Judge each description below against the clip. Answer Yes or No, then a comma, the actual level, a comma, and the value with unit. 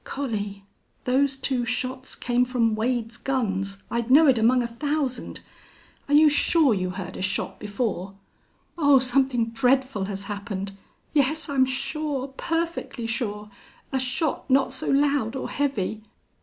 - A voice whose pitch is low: No, very high, 250 Hz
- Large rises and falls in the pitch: No, average, 4.1 semitones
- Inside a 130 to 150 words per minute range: Yes, average, 140 wpm